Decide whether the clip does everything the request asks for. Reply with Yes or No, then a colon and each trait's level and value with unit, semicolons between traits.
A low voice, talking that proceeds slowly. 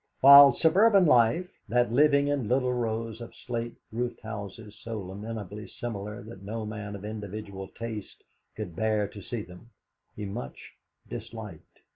No: low, 110 Hz; average, 145 wpm